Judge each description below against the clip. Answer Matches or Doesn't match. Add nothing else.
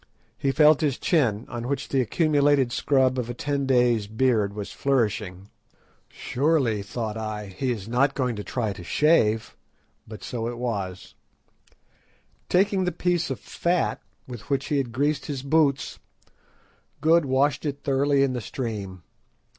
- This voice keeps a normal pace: Matches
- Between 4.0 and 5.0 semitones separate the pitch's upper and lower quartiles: Matches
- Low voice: Matches